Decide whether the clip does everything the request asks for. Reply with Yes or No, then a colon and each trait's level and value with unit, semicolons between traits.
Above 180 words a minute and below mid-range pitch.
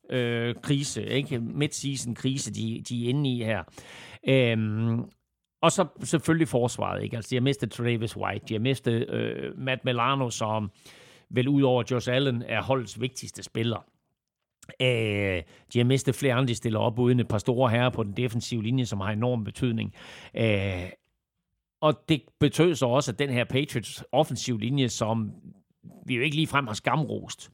No: average, 170 wpm; low, 125 Hz